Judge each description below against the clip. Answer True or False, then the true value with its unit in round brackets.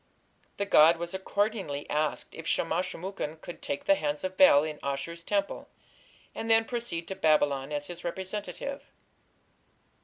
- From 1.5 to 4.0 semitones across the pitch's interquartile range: False (4.6 semitones)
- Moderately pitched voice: True (170 Hz)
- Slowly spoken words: False (155 wpm)